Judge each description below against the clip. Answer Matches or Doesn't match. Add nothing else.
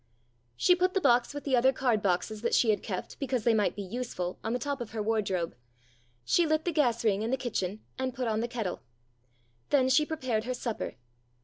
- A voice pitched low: Doesn't match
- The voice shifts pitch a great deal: Doesn't match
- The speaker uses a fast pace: Matches